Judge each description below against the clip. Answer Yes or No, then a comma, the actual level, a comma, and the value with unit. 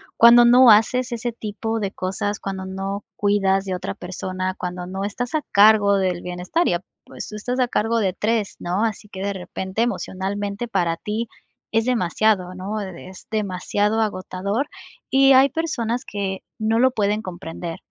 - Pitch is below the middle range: No, high, 205 Hz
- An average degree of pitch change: Yes, average, 3.2 semitones